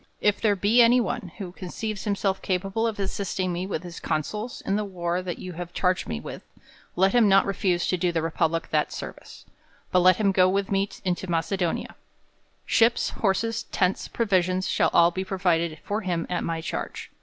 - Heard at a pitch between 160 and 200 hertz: Yes, medium, 185 Hz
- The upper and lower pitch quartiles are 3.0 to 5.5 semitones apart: No, narrow, 2.4 semitones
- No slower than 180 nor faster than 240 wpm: Yes, average, 195 wpm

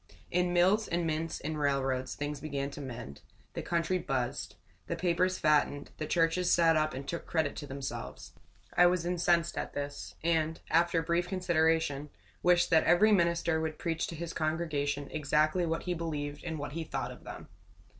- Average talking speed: Yes, average, 175 wpm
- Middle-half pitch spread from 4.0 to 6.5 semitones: No, average, 2.9 semitones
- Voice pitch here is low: No, medium, 160 Hz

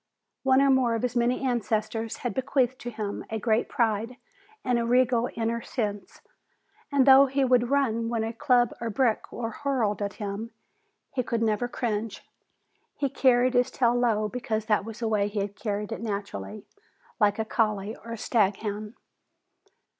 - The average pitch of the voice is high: Yes, high, 230 Hz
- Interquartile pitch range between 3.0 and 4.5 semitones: No, narrow, 2.6 semitones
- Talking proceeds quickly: No, average, 170 wpm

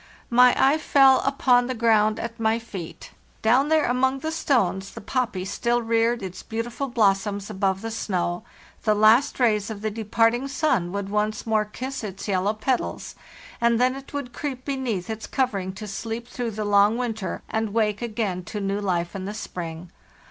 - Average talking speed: Yes, average, 180 wpm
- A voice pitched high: Yes, high, 225 Hz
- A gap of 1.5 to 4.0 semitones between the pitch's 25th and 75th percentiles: Yes, average, 3.5 semitones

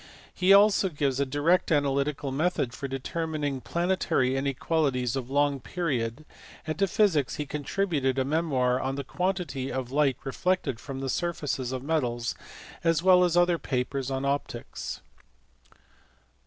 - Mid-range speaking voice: Yes, medium, 145 Hz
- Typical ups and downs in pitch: Yes, average, 4.1 semitones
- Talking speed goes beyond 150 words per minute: No, average, 140 wpm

